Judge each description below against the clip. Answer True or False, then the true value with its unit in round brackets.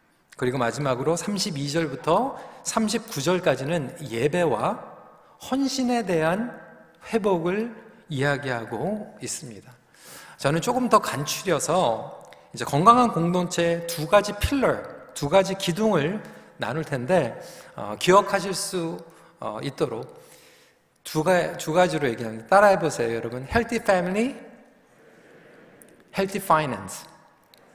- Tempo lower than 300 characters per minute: True (270 characters per minute)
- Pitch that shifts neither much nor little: False (6.6 semitones)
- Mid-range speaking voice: True (175 Hz)